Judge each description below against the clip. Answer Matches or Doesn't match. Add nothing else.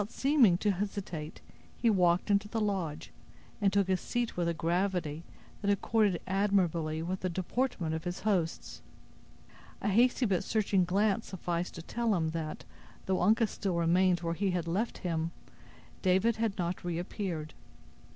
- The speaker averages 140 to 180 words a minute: Matches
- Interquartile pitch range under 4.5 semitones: Matches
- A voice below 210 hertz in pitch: Matches